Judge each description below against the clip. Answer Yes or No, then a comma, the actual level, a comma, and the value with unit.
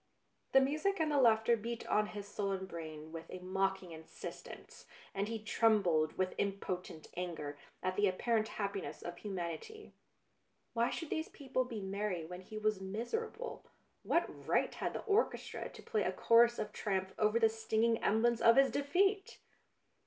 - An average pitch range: Yes, average, 4.2 semitones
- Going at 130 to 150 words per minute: No, average, 170 wpm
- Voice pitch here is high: Yes, high, 215 Hz